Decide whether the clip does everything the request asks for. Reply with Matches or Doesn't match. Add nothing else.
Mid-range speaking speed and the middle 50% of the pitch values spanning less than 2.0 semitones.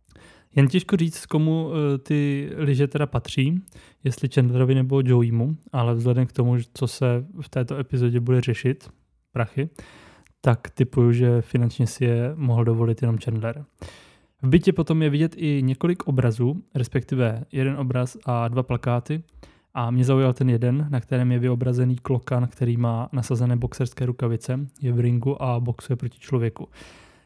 Doesn't match